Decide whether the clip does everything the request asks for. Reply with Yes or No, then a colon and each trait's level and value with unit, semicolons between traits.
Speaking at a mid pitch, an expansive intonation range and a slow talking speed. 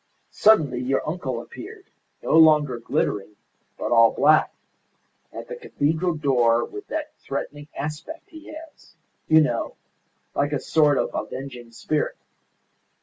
Yes: medium, 150 Hz; wide, 6.0 semitones; slow, 130 wpm